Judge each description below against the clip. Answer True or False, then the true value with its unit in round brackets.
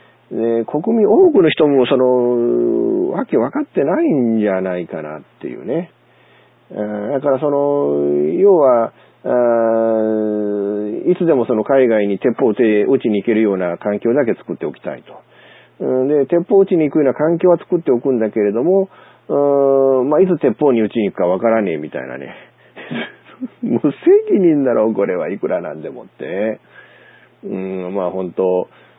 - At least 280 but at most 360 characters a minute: True (300 characters per minute)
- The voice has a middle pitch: False (120 Hz)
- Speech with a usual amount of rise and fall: False (5.7 semitones)